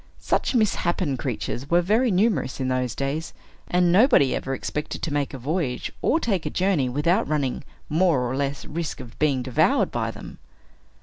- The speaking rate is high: No, average, 175 wpm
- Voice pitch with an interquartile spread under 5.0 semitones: No, average, 5.3 semitones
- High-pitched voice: No, medium, 150 Hz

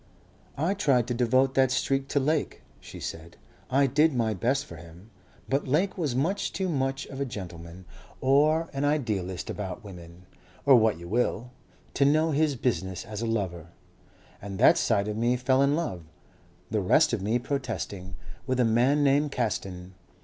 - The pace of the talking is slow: No, average, 175 wpm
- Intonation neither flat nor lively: No, wide, 6.2 semitones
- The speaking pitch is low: Yes, low, 125 Hz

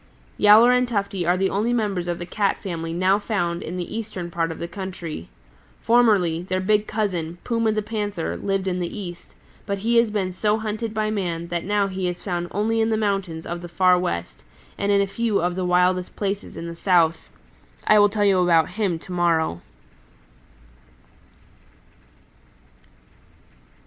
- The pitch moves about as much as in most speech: Yes, average, 3.3 semitones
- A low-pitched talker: No, high, 190 Hz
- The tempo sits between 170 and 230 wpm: Yes, average, 180 wpm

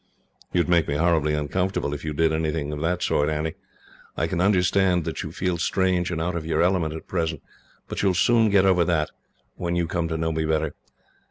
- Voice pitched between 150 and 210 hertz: No, very low, 85 Hz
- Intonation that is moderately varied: No, narrow, 2.3 semitones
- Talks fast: Yes, fast, 225 wpm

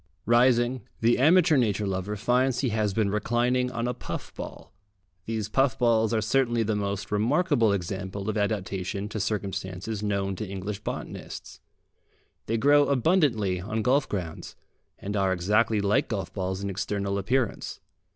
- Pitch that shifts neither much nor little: Yes, average, 3.5 semitones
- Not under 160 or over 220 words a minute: No, average, 150 wpm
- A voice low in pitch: Yes, low, 105 Hz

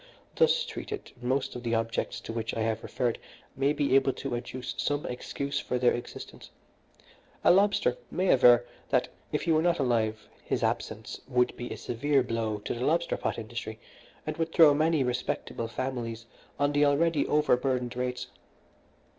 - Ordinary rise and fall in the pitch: Yes, average, 3.6 semitones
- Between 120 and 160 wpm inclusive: No, average, 170 wpm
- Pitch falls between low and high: No, low, 125 Hz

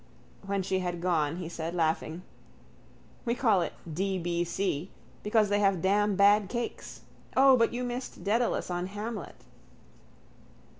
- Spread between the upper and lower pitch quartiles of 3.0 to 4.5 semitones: Yes, average, 3.5 semitones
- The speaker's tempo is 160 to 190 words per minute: No, slow, 135 wpm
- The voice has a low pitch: No, high, 195 Hz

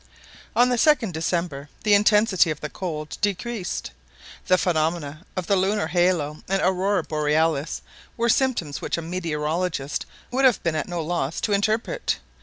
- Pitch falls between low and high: Yes, medium, 175 Hz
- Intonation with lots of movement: No, average, 4.7 semitones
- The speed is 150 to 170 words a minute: Yes, average, 155 wpm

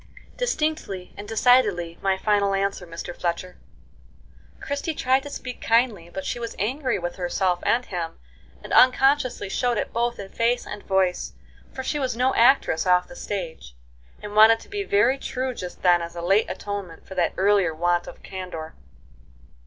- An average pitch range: No, wide, 5.8 semitones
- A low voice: No, high, 205 Hz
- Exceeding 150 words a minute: Yes, average, 170 wpm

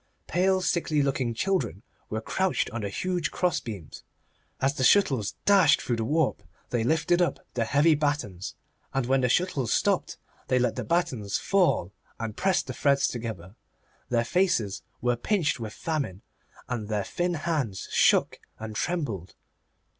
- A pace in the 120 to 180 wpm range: Yes, average, 155 wpm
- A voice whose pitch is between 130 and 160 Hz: Yes, low, 135 Hz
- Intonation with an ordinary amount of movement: No, wide, 7.4 semitones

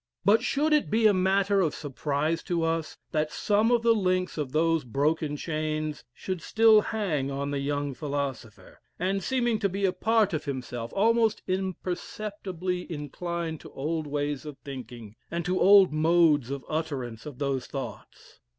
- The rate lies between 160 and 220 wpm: Yes, average, 165 wpm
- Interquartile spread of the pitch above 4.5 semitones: Yes, average, 5.3 semitones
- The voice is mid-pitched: Yes, medium, 165 Hz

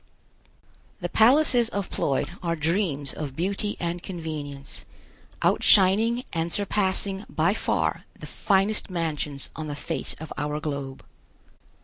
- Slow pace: Yes, slow, 120 wpm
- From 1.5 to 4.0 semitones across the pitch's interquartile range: No, average, 5.2 semitones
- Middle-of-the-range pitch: Yes, medium, 170 Hz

